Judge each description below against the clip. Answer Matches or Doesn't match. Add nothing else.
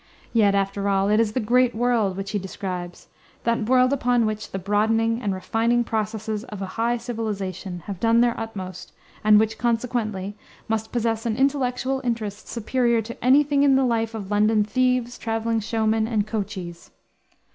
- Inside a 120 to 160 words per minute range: Doesn't match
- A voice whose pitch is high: Matches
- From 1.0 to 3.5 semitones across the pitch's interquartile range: Matches